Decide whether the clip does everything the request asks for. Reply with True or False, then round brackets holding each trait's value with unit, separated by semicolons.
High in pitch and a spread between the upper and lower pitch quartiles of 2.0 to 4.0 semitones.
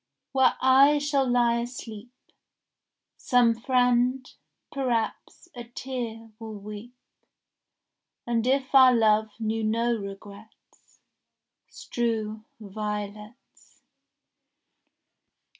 True (235 Hz; 2.7 semitones)